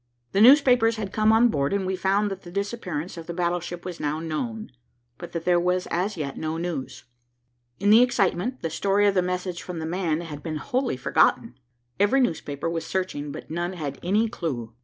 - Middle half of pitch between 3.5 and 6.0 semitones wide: Yes, average, 4.0 semitones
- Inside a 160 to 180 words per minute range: No, average, 200 wpm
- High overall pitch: No, medium, 180 Hz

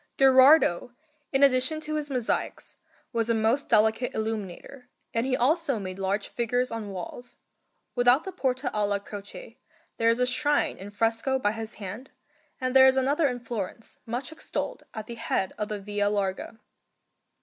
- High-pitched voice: Yes, high, 235 Hz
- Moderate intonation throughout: Yes, average, 3.9 semitones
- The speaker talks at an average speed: Yes, average, 165 wpm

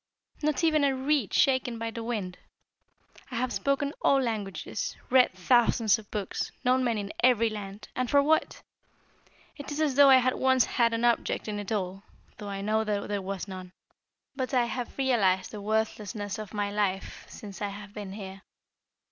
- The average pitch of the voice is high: Yes, high, 220 Hz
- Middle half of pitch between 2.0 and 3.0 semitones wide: No, average, 4.2 semitones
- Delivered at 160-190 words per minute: Yes, average, 185 wpm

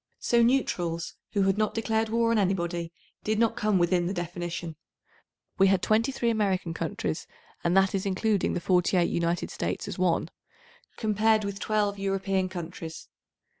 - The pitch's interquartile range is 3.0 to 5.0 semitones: Yes, average, 3.6 semitones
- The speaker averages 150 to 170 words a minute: Yes, average, 160 wpm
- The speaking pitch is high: Yes, high, 195 Hz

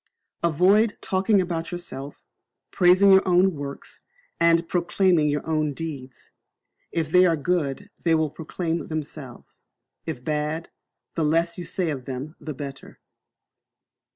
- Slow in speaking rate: Yes, slow, 130 wpm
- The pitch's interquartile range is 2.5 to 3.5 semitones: Yes, average, 3.0 semitones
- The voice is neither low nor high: Yes, medium, 165 Hz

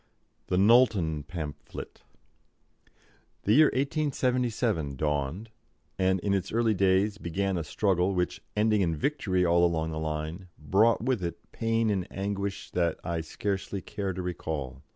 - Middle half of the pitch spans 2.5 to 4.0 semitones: No, average, 4.4 semitones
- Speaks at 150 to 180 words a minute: No, average, 140 wpm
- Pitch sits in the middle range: No, very low, 95 Hz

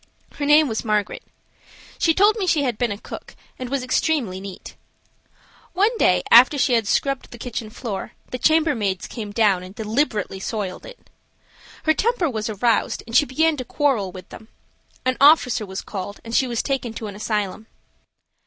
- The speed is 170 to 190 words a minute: Yes, average, 180 wpm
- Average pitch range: No, wide, 5.7 semitones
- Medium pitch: No, high, 235 Hz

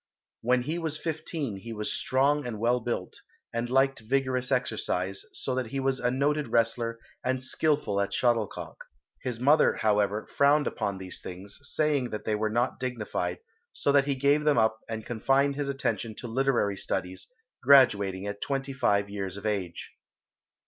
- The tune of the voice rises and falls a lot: No, average, 4.5 semitones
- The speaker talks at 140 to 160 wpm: No, average, 170 wpm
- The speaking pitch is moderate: No, low, 120 Hz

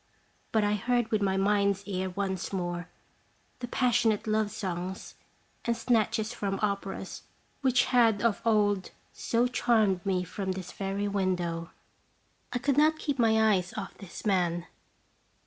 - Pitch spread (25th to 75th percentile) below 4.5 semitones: Yes, average, 3.4 semitones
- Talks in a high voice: Yes, high, 205 Hz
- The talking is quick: No, average, 145 wpm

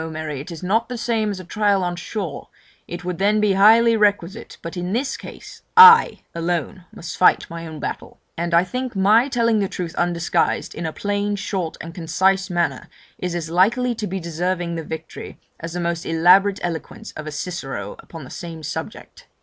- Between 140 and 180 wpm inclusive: No, average, 195 wpm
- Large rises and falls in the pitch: No, average, 3.6 semitones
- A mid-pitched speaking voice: Yes, medium, 180 Hz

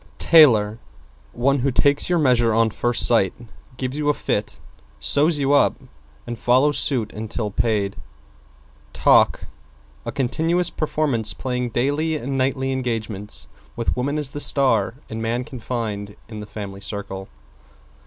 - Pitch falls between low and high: No, low, 125 Hz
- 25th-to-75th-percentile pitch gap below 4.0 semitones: No, average, 4.3 semitones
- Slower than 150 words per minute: Yes, average, 140 wpm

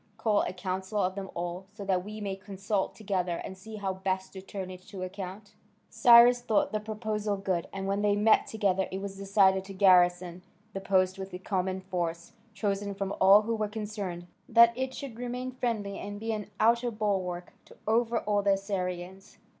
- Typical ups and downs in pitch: No, narrow, 2.2 semitones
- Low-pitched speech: No, high, 195 Hz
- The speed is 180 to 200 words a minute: Yes, average, 190 wpm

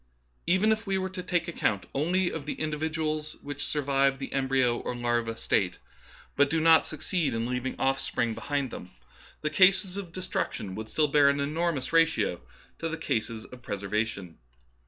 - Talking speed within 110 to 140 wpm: No, average, 180 wpm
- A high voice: No, medium, 145 Hz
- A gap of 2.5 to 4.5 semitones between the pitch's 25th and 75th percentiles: No, wide, 5.5 semitones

